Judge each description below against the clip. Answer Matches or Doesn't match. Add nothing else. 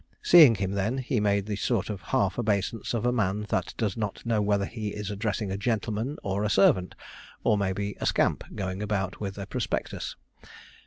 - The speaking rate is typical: Matches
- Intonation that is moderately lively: Doesn't match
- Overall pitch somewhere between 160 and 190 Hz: Doesn't match